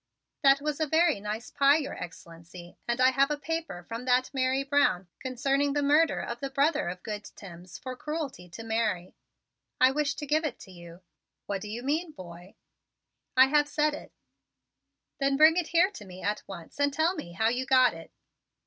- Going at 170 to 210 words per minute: Yes, average, 195 wpm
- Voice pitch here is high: Yes, very high, 260 Hz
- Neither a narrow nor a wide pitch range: No, wide, 6.6 semitones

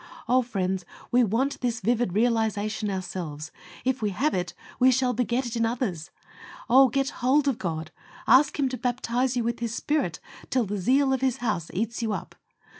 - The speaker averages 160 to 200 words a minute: Yes, average, 190 wpm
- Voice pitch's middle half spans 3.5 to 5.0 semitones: Yes, average, 4.1 semitones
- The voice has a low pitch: No, high, 235 Hz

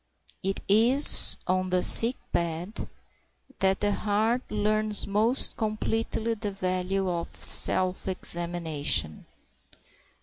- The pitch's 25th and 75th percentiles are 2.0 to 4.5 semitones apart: Yes, average, 2.9 semitones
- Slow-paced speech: Yes, slow, 100 wpm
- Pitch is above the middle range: Yes, high, 195 Hz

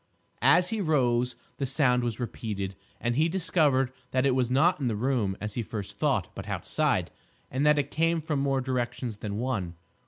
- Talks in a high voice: No, low, 130 Hz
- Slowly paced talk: No, average, 190 wpm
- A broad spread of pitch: No, average, 4.1 semitones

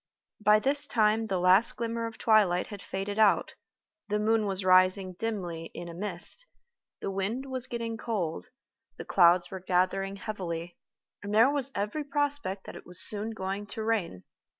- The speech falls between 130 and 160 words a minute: No, average, 170 wpm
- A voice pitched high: Yes, high, 205 Hz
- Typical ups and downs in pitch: Yes, average, 3.5 semitones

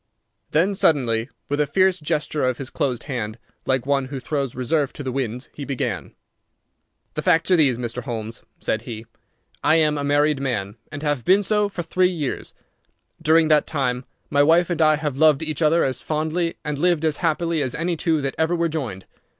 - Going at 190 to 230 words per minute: Yes, average, 200 wpm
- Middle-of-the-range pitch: Yes, medium, 150 Hz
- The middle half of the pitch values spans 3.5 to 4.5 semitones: Yes, average, 3.8 semitones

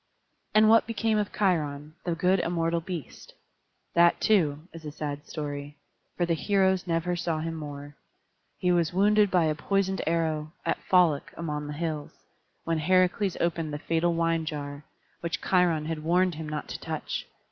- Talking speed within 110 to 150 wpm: No, average, 170 wpm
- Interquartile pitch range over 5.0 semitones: No, average, 3.0 semitones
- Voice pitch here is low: No, medium, 165 Hz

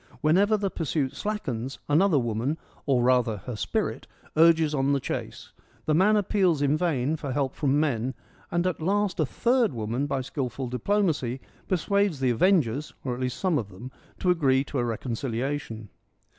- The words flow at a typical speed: Yes, average, 185 wpm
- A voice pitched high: No, medium, 140 Hz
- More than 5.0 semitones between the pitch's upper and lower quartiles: Yes, wide, 5.5 semitones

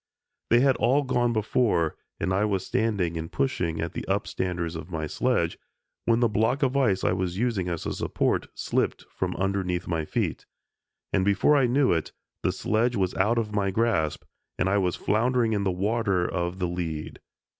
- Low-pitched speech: Yes, low, 100 Hz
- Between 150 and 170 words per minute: No, average, 190 wpm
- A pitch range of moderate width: Yes, average, 5.0 semitones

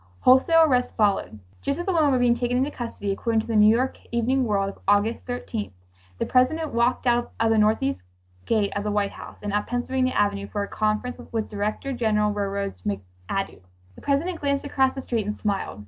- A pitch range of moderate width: Yes, average, 3.9 semitones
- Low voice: No, high, 225 Hz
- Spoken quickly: Yes, fast, 210 wpm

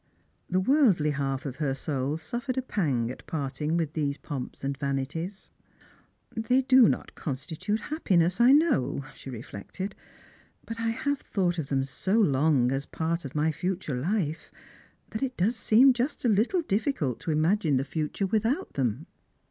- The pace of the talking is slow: No, average, 175 wpm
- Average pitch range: No, wide, 8.2 semitones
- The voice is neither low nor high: Yes, medium, 165 Hz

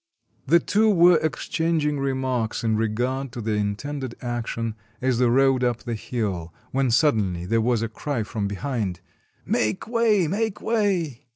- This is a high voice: No, low, 125 Hz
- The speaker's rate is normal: Yes, average, 160 wpm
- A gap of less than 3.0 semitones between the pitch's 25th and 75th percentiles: No, average, 5.2 semitones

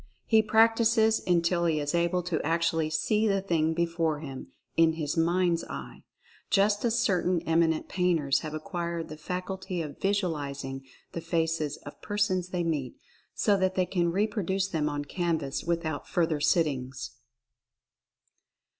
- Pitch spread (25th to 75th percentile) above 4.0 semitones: No, average, 3.2 semitones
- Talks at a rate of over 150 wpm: No, average, 145 wpm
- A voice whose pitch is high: No, medium, 170 Hz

